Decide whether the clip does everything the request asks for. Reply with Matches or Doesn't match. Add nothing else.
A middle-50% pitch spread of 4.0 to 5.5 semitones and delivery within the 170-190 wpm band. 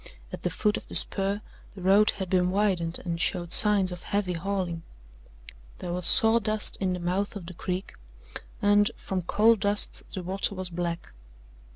Doesn't match